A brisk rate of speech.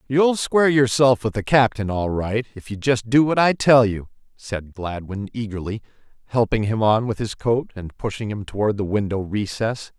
No: average, 190 wpm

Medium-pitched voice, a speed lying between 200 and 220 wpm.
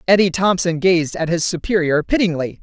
No: medium, 175 Hz; average, 160 wpm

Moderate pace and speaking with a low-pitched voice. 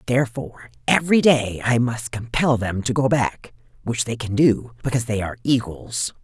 Yes: average, 175 wpm; low, 120 Hz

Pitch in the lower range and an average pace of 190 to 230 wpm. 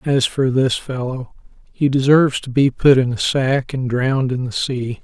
Yes: low, 130 Hz; average, 200 wpm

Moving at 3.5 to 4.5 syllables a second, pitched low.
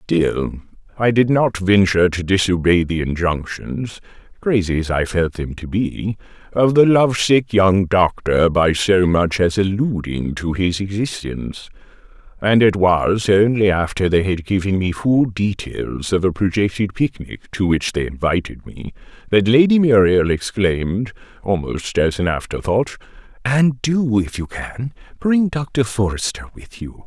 Yes: 4.3 syllables/s; low, 100 Hz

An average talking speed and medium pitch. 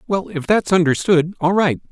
Yes: average, 190 wpm; medium, 175 Hz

